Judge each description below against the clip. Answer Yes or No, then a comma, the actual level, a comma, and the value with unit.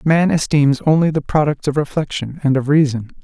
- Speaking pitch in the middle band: Yes, medium, 145 Hz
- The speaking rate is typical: Yes, average, 185 wpm